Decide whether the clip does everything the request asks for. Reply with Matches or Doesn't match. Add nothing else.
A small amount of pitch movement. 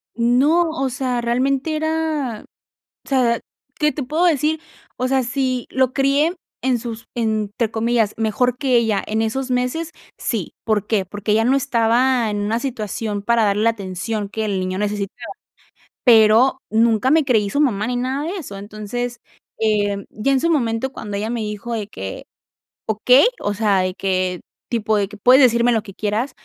Doesn't match